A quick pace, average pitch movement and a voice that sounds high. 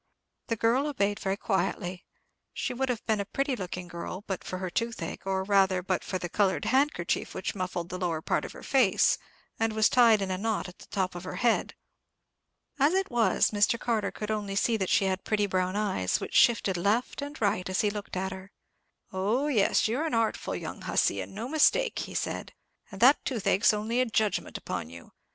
Yes: fast, 210 wpm; average, 3.7 semitones; high, 205 Hz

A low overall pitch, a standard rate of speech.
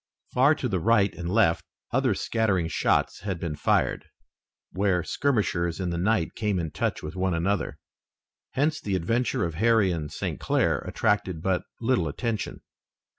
Yes: very low, 95 Hz; average, 160 wpm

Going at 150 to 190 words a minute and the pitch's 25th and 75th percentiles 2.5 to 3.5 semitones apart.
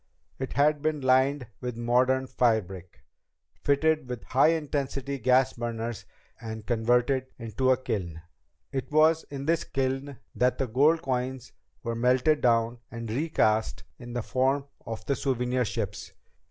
No: average, 140 wpm; average, 2.9 semitones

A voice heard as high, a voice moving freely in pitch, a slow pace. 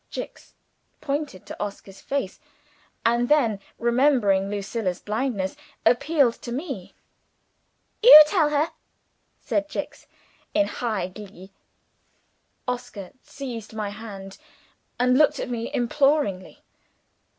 Yes: high, 235 Hz; wide, 5.8 semitones; slow, 105 wpm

